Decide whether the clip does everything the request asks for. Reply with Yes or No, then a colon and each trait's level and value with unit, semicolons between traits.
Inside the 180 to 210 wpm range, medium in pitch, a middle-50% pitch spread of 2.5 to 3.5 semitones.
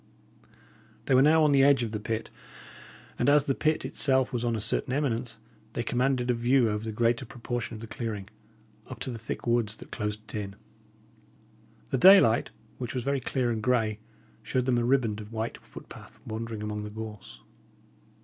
No: average, 190 wpm; low, 120 Hz; average, 3.0 semitones